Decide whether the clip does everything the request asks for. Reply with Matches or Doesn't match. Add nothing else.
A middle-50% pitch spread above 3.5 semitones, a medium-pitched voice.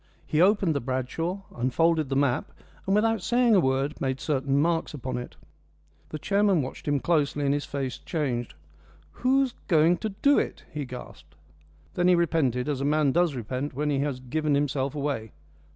Matches